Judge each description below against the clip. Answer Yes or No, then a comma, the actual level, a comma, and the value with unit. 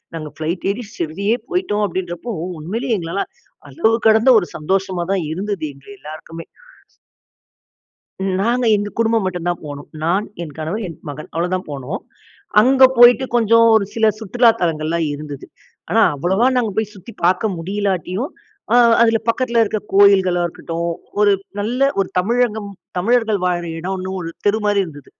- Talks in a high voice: Yes, high, 195 Hz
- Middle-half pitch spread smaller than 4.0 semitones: No, average, 4.8 semitones